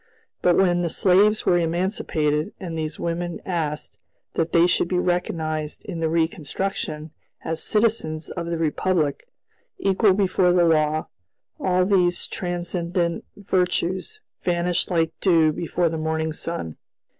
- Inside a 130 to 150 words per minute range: Yes, slow, 135 wpm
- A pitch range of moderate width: No, narrow, 2.3 semitones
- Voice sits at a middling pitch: Yes, medium, 170 Hz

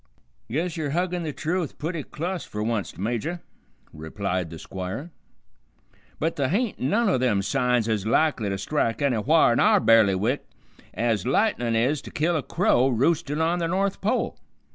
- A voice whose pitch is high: No, medium, 140 Hz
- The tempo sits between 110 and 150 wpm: No, average, 165 wpm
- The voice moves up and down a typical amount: No, wide, 7.0 semitones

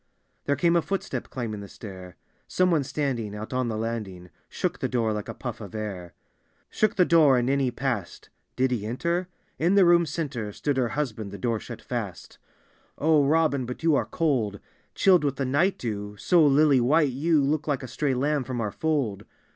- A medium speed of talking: No, fast, 210 wpm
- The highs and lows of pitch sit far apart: Yes, wide, 5.8 semitones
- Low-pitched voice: Yes, low, 130 Hz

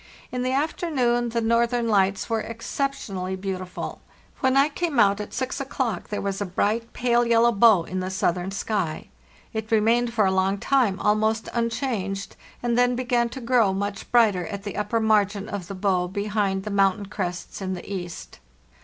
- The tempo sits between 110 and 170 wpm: No, average, 180 wpm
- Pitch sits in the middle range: No, high, 215 Hz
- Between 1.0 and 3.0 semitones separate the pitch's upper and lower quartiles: No, average, 3.5 semitones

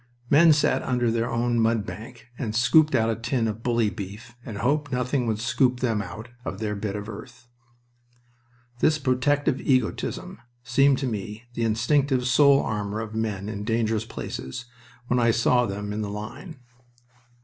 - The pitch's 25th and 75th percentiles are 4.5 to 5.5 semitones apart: No, average, 2.9 semitones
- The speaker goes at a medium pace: Yes, average, 170 wpm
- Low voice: Yes, low, 115 Hz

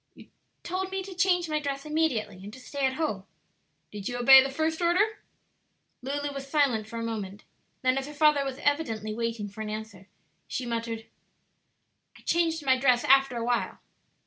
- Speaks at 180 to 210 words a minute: Yes, average, 185 wpm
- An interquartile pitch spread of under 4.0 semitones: No, average, 5.1 semitones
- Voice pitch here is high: Yes, very high, 270 Hz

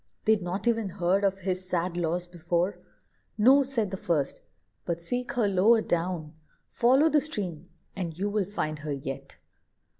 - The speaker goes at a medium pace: Yes, average, 160 wpm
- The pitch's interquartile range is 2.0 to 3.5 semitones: No, average, 4.0 semitones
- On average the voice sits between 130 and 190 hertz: Yes, medium, 185 Hz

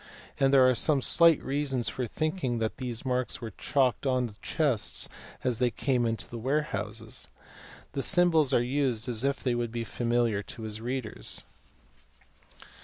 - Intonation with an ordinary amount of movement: Yes, average, 3.0 semitones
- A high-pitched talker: No, low, 125 Hz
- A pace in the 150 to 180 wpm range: Yes, average, 170 wpm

